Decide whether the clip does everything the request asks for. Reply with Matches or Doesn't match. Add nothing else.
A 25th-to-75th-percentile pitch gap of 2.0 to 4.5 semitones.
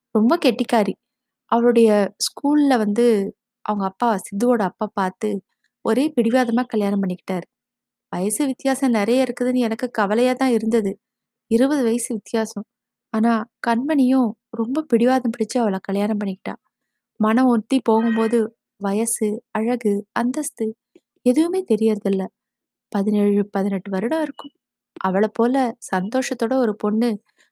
Matches